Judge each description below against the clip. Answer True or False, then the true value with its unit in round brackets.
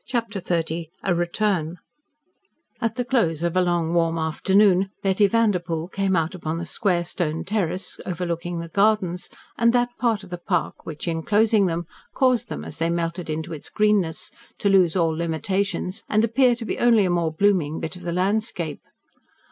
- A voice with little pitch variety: False (3.8 semitones)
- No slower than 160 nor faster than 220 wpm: True (175 wpm)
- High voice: False (180 Hz)